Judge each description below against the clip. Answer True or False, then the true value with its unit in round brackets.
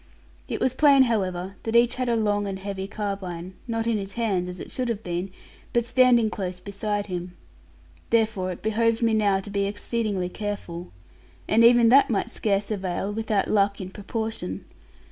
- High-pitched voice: True (205 Hz)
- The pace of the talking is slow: False (180 wpm)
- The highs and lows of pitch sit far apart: False (3.0 semitones)